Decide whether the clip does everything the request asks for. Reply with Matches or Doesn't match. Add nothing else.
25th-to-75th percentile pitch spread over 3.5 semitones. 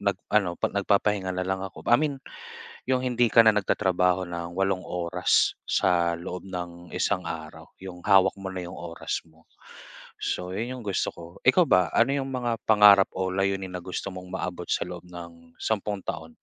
Doesn't match